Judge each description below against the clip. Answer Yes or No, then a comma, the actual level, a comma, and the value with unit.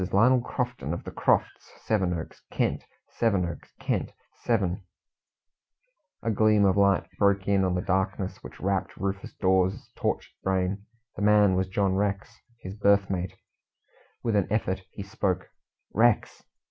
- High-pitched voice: No, low, 100 Hz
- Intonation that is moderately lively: No, narrow, 2.0 semitones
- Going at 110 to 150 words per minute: Yes, average, 145 wpm